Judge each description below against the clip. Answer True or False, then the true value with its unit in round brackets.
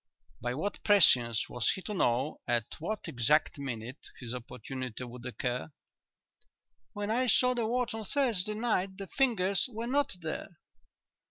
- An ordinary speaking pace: True (150 wpm)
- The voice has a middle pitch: True (180 Hz)